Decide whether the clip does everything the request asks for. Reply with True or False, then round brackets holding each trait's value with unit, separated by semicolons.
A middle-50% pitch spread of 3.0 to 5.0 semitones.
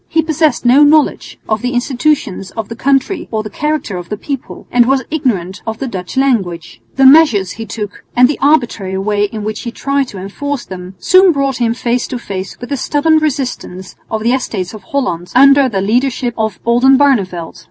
False (5.4 semitones)